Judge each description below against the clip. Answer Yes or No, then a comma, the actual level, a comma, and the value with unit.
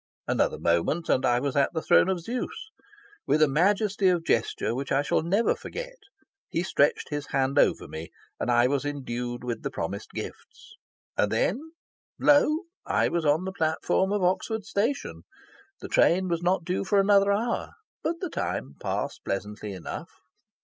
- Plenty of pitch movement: Yes, wide, 7.5 semitones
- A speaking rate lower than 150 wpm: No, average, 170 wpm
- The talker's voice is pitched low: No, medium, 165 Hz